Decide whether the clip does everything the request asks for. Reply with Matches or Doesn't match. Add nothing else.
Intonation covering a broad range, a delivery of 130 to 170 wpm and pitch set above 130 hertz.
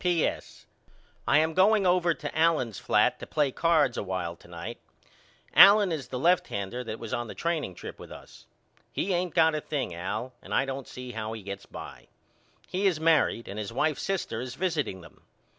Doesn't match